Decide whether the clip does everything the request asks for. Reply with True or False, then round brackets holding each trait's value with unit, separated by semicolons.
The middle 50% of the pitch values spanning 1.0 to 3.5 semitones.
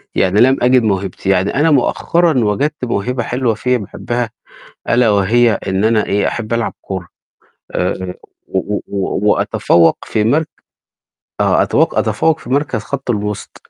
False (4.1 semitones)